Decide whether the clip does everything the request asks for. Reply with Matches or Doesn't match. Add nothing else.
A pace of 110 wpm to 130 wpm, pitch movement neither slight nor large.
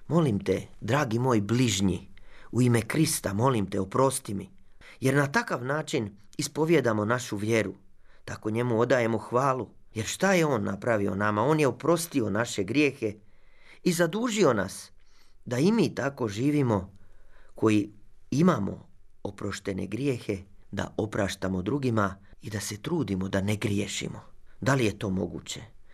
Doesn't match